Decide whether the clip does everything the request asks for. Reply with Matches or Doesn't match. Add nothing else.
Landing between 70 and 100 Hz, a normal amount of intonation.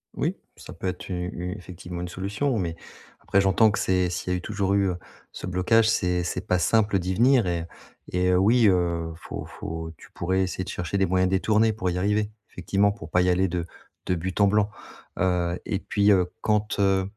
Doesn't match